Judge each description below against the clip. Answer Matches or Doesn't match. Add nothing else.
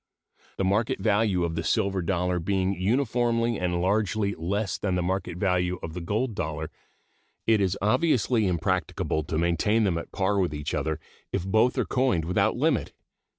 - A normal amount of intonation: Matches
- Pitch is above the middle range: Doesn't match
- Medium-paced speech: Matches